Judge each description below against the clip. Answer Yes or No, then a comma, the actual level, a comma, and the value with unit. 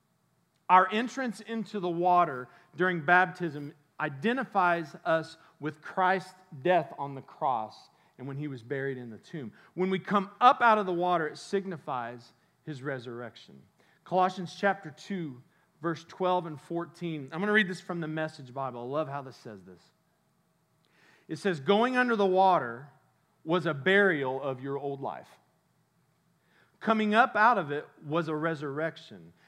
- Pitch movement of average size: Yes, average, 4.3 semitones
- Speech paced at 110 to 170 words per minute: Yes, average, 160 wpm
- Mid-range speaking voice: Yes, medium, 165 Hz